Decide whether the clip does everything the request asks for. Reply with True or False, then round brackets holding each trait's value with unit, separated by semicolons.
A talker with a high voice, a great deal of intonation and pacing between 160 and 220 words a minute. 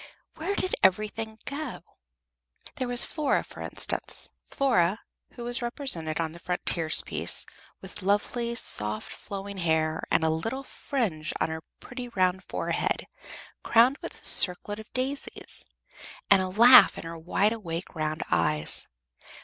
False (200 Hz; 6.7 semitones; 140 wpm)